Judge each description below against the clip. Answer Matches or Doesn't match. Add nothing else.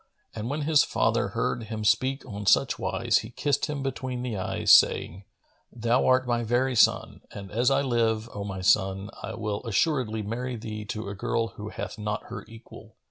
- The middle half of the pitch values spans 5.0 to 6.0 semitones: Doesn't match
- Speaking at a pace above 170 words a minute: Matches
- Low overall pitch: Matches